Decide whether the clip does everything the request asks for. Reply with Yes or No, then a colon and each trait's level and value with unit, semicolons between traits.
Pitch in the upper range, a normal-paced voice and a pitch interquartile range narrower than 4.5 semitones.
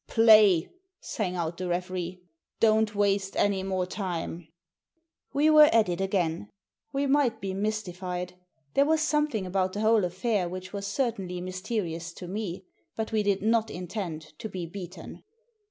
Yes: high, 195 Hz; average, 155 wpm; average, 3.4 semitones